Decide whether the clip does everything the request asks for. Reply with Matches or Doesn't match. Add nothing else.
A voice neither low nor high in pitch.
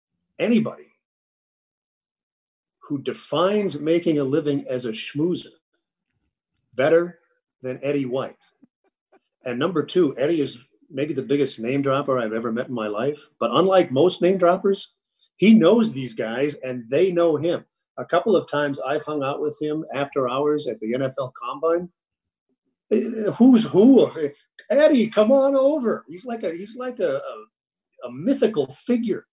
Matches